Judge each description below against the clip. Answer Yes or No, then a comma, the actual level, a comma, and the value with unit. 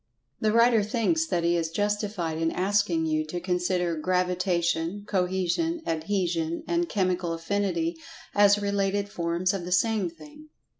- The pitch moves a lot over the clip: No, average, 3.3 semitones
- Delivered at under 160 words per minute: Yes, average, 140 wpm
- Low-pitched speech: No, medium, 185 Hz